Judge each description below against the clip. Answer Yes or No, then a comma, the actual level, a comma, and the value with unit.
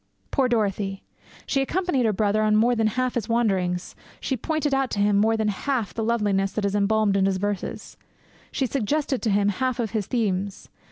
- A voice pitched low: No, high, 215 Hz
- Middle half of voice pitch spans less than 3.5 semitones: No, average, 3.8 semitones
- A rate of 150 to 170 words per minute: No, average, 190 wpm